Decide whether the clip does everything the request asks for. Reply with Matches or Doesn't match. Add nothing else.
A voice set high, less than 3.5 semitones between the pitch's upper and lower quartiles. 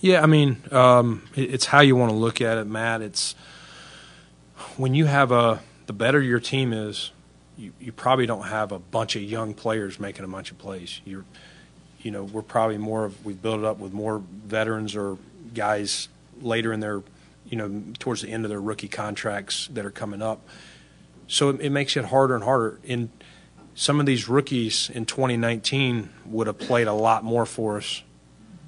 Doesn't match